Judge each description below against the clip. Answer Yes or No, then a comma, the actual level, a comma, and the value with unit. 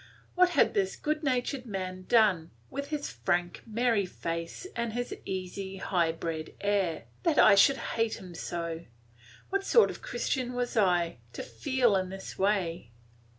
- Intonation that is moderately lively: No, wide, 6.0 semitones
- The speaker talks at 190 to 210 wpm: No, average, 155 wpm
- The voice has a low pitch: No, high, 200 Hz